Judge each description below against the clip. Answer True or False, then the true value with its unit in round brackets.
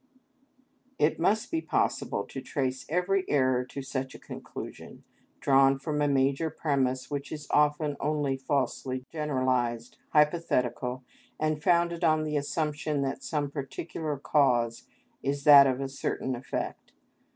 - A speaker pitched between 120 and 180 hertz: True (140 Hz)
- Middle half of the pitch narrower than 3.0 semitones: True (2.5 semitones)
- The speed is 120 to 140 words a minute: True (135 wpm)